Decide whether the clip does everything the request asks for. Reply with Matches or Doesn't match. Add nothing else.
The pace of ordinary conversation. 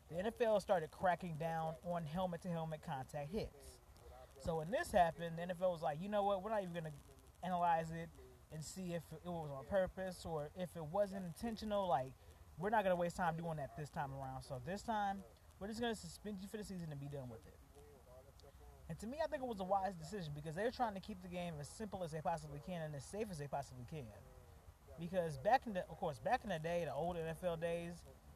Doesn't match